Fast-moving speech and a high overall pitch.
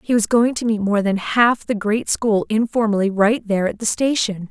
Yes: fast, 225 wpm; high, 215 Hz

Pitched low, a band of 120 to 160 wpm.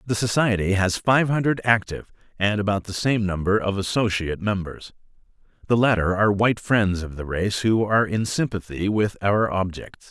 No: low, 100 Hz; average, 170 wpm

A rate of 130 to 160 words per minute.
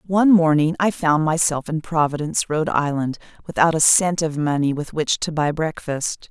No: average, 180 wpm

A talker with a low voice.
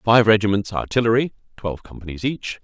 Yes: low, 105 Hz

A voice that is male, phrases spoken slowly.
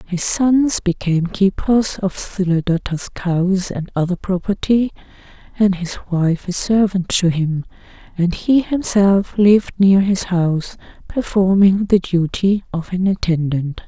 No: female; slow, 130 wpm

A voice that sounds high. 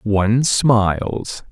No: low, 110 Hz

